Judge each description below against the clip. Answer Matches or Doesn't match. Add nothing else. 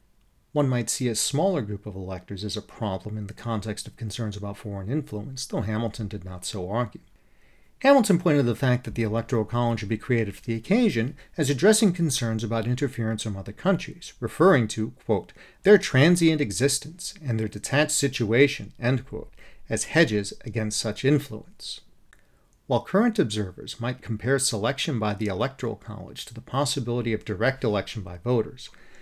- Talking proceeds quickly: Doesn't match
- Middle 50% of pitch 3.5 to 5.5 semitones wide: Matches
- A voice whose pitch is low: Matches